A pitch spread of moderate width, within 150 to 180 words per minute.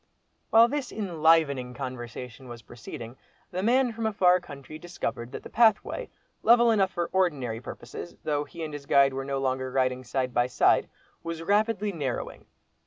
No: wide, 7.1 semitones; average, 170 wpm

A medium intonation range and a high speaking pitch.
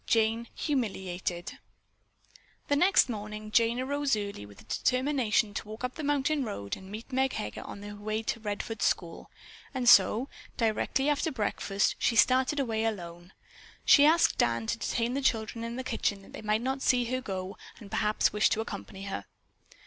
Yes: average, 4.1 semitones; high, 225 Hz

